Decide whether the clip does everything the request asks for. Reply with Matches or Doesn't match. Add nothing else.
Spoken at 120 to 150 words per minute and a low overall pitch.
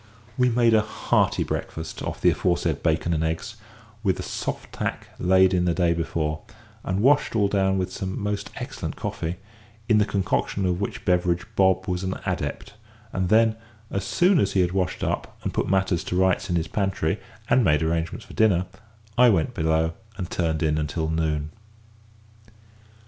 Doesn't match